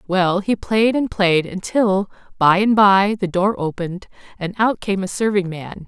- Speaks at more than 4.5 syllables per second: No, 4.4 syllables/s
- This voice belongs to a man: No, female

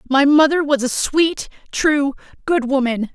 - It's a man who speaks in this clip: No, female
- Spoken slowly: No, average, 155 wpm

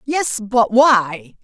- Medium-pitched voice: No, high, 230 Hz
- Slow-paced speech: Yes, slow, 125 wpm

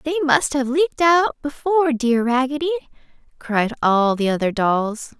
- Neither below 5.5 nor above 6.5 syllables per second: No, 5.0 syllables/s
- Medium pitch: No, very high, 270 Hz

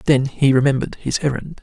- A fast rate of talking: No, average, 185 wpm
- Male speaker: Yes, male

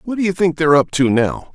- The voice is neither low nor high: Yes, medium, 165 Hz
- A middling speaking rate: No, fast, 310 wpm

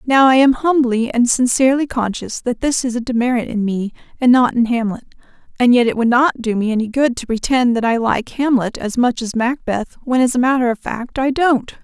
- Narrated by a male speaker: No, female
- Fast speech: Yes, fast, 230 wpm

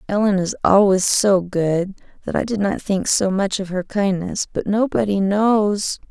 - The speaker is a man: No, female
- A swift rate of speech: No, average, 175 wpm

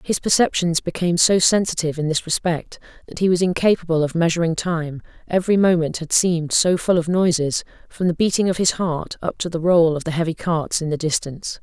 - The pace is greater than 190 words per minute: Yes, fast, 205 wpm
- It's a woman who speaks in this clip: Yes, female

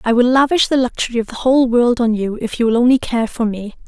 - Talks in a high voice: Yes, high, 240 Hz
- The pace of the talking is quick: Yes, fast, 280 wpm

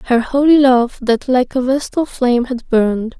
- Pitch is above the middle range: Yes, very high, 250 Hz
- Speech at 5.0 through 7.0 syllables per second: No, 4.8 syllables/s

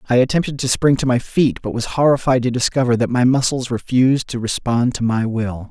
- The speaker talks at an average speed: No, fast, 220 wpm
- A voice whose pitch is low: Yes, low, 125 Hz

